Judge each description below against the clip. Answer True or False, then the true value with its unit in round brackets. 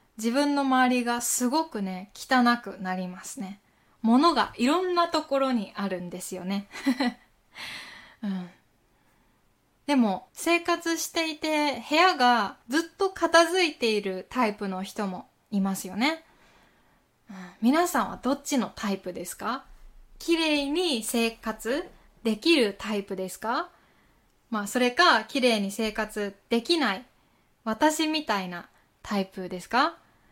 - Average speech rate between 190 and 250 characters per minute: True (240 characters per minute)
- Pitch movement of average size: False (7.2 semitones)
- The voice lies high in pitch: True (240 Hz)